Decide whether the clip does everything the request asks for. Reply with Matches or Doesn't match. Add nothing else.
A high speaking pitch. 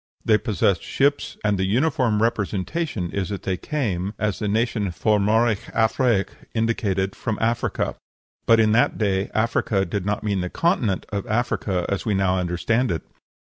Doesn't match